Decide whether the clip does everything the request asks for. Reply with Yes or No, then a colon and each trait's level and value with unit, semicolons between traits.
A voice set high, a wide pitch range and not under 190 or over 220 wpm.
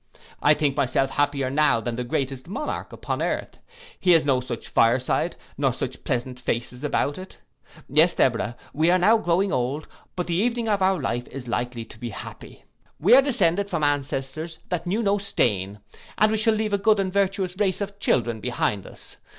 No: medium, 150 Hz; wide, 7.6 semitones; average, 195 wpm